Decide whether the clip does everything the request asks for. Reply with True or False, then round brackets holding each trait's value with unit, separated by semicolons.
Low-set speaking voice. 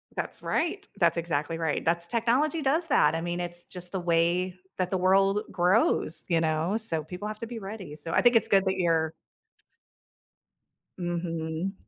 False (180 Hz)